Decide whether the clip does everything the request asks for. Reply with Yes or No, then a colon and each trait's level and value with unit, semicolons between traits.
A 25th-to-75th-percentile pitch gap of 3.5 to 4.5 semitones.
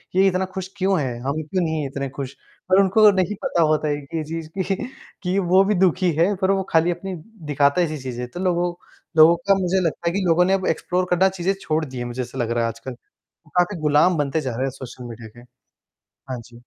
No: average, 5.3 semitones